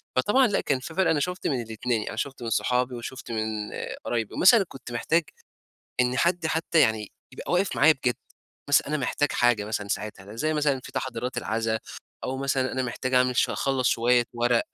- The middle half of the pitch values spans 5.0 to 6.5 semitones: No, average, 4.0 semitones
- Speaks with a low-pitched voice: Yes, low, 125 Hz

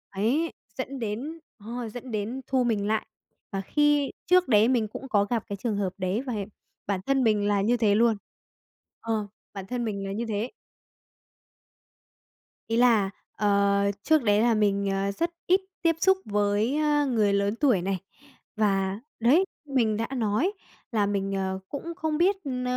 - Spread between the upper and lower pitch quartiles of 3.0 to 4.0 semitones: No, average, 4.5 semitones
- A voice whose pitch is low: No, high, 220 Hz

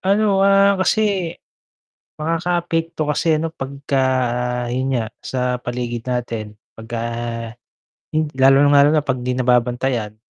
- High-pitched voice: No, low, 135 Hz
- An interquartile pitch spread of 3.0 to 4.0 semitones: No, average, 5.0 semitones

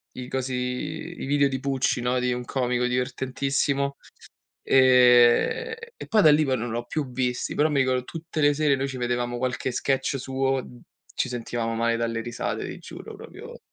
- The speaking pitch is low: Yes, low, 130 Hz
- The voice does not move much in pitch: Yes, narrow, 2.1 semitones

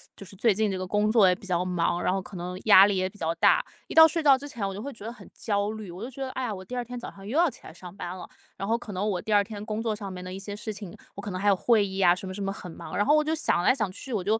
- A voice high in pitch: Yes, high, 205 Hz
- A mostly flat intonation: No, average, 3.3 semitones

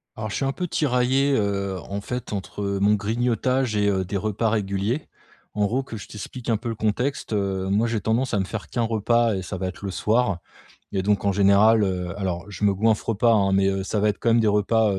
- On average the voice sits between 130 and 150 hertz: No, low, 105 Hz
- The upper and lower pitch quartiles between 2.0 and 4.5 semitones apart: Yes, average, 2.8 semitones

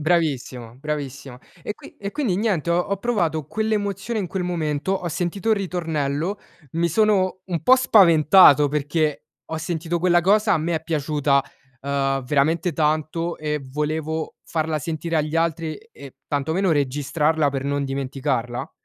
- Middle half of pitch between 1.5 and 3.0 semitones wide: No, average, 3.7 semitones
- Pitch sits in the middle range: Yes, medium, 160 Hz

